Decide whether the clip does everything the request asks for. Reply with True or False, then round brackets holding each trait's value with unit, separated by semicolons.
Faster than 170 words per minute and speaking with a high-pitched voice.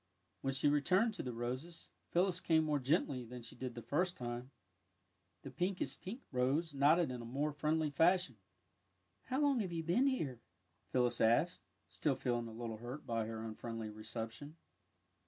False (185 wpm; 135 Hz)